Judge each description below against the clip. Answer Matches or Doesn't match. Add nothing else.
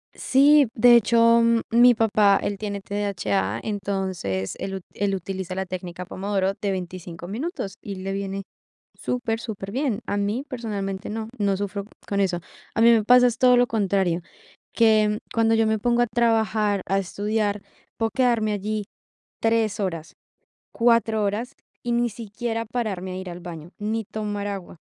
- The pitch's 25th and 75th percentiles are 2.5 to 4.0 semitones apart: Matches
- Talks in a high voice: Matches